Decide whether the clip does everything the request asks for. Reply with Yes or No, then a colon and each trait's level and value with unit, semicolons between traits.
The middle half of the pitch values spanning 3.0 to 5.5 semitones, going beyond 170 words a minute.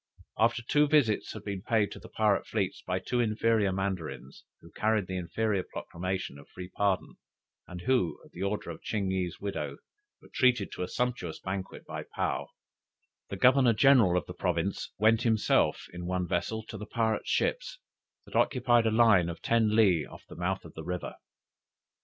Yes: average, 3.7 semitones; average, 180 wpm